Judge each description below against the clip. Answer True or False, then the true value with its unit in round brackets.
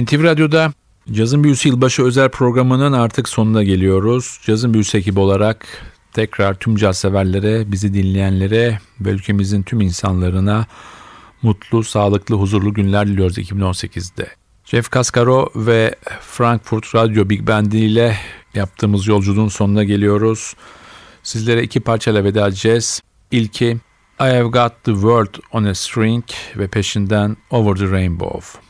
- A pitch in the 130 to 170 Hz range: False (110 Hz)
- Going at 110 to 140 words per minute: True (130 wpm)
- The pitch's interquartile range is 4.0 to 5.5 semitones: False (2.6 semitones)